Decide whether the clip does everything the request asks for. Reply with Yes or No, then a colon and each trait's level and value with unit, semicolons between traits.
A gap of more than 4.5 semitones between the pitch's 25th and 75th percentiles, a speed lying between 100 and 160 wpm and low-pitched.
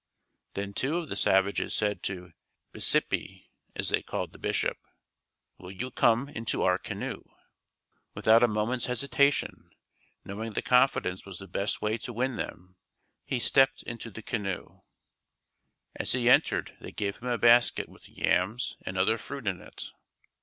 No: average, 4.2 semitones; average, 155 wpm; low, 110 Hz